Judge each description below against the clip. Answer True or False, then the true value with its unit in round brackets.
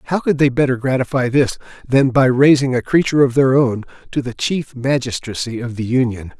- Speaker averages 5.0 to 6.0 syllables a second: True (5.5 syllables/s)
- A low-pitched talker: True (130 Hz)